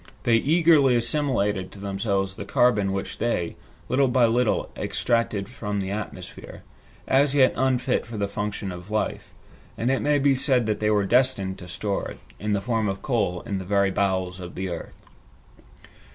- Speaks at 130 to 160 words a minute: No, average, 180 wpm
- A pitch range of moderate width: Yes, average, 4.4 semitones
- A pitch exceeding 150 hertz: No, low, 105 Hz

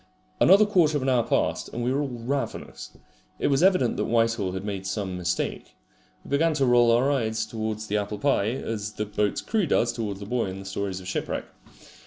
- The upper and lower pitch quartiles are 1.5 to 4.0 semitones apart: No, average, 4.9 semitones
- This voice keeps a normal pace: No, fast, 215 wpm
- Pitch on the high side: No, low, 115 Hz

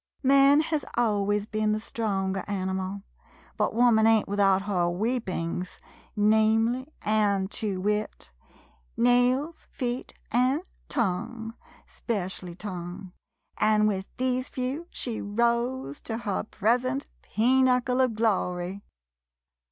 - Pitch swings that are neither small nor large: Yes, average, 4.0 semitones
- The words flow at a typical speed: No, slow, 115 wpm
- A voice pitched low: No, high, 220 Hz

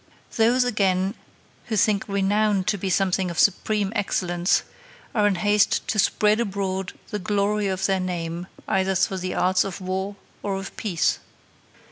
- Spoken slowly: No, average, 155 wpm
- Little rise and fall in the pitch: Yes, narrow, 2.0 semitones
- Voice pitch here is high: Yes, high, 195 Hz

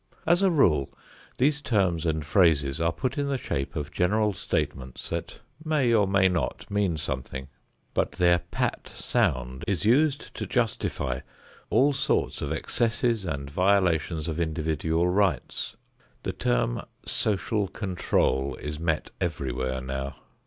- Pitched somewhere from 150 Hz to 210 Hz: No, very low, 85 Hz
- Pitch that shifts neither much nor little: No, wide, 6.9 semitones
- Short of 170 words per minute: Yes, average, 140 wpm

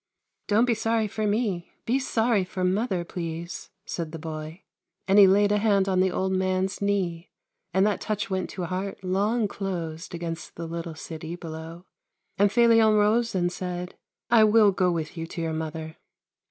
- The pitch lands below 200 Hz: Yes, medium, 185 Hz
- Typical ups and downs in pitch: Yes, average, 3.6 semitones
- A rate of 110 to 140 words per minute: No, average, 190 wpm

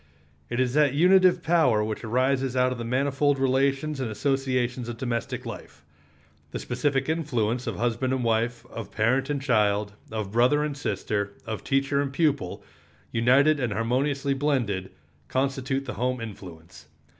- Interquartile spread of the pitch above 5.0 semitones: No, average, 3.2 semitones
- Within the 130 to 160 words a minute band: Yes, average, 155 wpm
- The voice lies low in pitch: Yes, low, 130 Hz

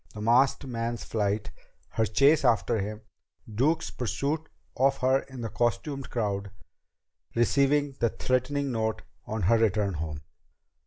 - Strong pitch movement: No, average, 4.2 semitones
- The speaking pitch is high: No, low, 120 Hz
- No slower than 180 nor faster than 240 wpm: No, average, 140 wpm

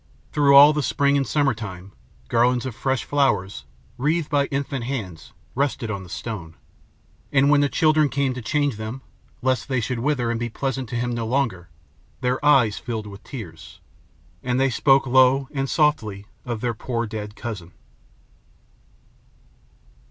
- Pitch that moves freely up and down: No, average, 4.2 semitones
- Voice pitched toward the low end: Yes, low, 125 Hz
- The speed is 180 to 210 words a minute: No, average, 160 wpm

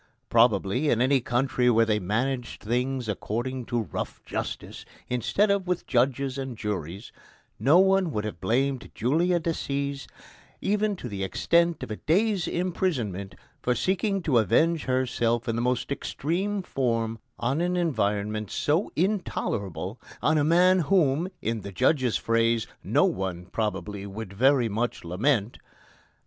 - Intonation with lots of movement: Yes, wide, 6.7 semitones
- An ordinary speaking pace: Yes, average, 145 wpm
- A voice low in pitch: Yes, low, 125 Hz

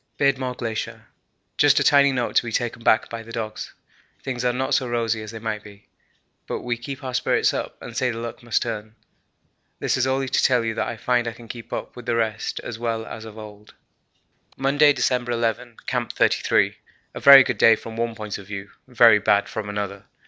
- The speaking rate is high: Yes, fast, 215 wpm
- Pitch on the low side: Yes, low, 115 Hz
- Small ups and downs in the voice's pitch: Yes, narrow, 2.2 semitones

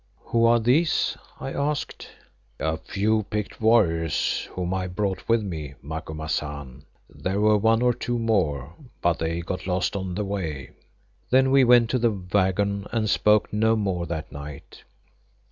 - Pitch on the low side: Yes, low, 100 Hz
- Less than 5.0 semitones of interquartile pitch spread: No, average, 5.3 semitones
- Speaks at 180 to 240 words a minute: No, average, 155 wpm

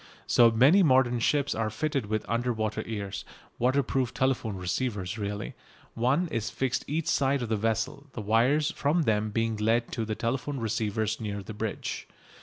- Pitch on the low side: Yes, low, 115 Hz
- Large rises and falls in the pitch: No, average, 3.5 semitones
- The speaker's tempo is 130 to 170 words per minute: Yes, average, 165 wpm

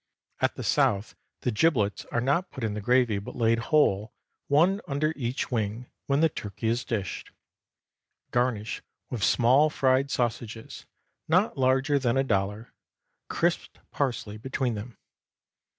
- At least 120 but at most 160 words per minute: Yes, average, 140 wpm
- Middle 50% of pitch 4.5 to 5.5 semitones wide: No, average, 4.0 semitones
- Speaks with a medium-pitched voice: No, low, 120 Hz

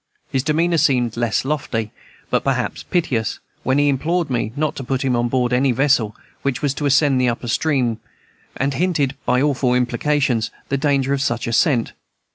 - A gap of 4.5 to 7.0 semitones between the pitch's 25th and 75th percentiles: No, average, 3.0 semitones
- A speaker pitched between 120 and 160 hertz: Yes, low, 135 Hz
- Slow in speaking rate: No, average, 180 wpm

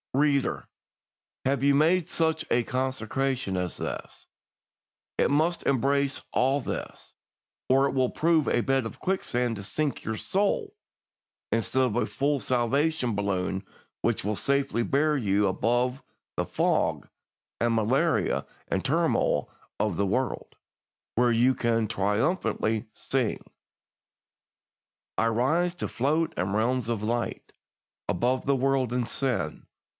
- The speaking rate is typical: No, slow, 130 wpm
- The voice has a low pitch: Yes, low, 130 Hz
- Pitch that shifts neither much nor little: Yes, average, 3.8 semitones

